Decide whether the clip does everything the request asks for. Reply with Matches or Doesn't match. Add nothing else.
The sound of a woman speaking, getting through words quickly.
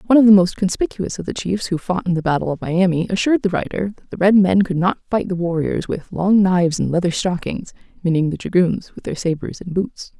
Matches